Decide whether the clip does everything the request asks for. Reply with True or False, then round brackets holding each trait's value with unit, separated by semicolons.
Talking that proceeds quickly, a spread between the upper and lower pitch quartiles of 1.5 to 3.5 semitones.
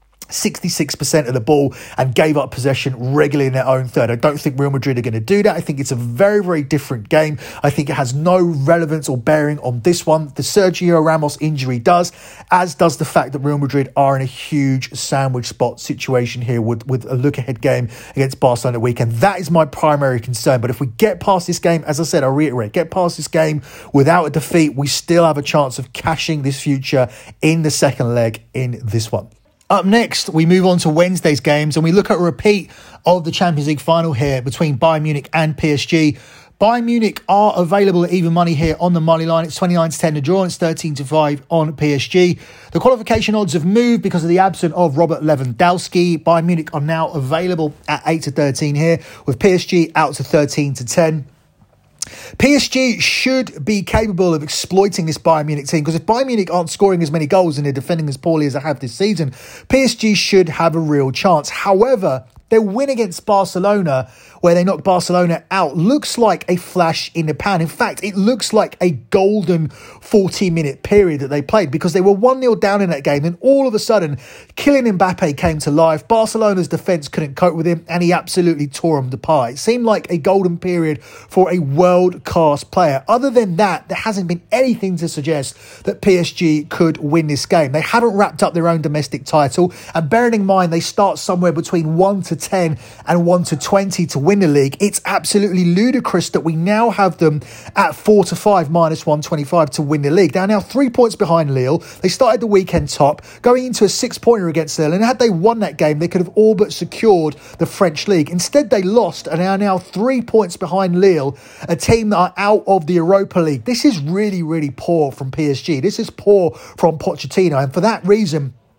False (215 wpm; 4.7 semitones)